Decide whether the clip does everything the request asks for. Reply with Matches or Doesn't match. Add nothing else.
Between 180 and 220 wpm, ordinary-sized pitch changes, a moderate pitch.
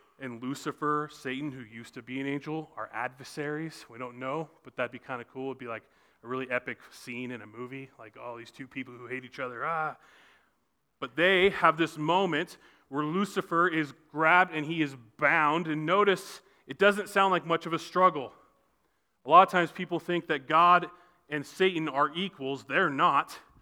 Matches